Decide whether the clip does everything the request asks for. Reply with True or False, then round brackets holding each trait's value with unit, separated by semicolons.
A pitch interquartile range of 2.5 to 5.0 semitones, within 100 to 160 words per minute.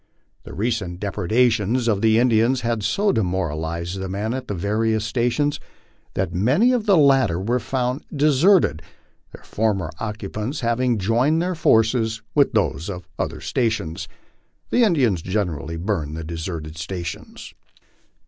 False (5.6 semitones; 140 wpm)